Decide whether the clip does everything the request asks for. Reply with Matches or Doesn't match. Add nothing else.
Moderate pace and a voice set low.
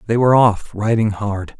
Matches